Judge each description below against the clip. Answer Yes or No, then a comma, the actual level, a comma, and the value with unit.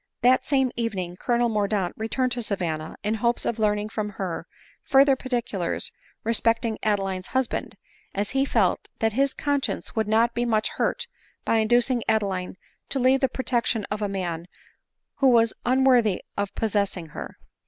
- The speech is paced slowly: No, average, 165 wpm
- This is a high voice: Yes, high, 220 Hz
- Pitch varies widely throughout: No, average, 3.5 semitones